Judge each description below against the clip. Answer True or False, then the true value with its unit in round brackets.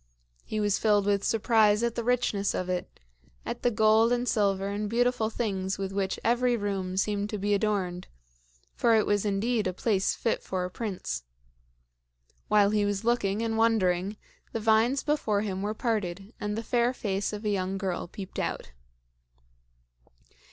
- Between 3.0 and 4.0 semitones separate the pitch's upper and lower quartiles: False (2.6 semitones)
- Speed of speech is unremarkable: True (170 wpm)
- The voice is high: True (210 Hz)